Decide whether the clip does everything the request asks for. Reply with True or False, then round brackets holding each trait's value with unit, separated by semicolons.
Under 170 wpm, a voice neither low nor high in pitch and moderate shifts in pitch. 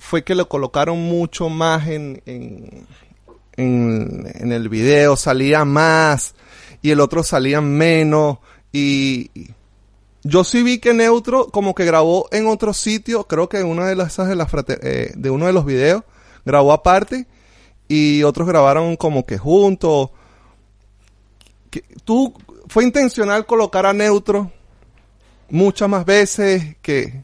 False (145 wpm; 155 Hz; 7.3 semitones)